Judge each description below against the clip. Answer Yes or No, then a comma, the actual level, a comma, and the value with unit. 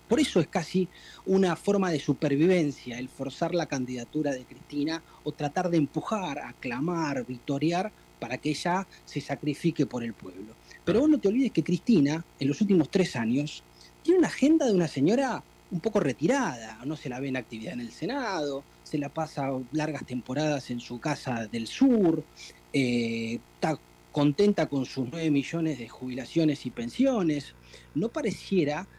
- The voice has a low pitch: No, medium, 150 Hz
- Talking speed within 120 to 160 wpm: No, average, 170 wpm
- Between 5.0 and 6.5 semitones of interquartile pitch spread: Yes, wide, 5.5 semitones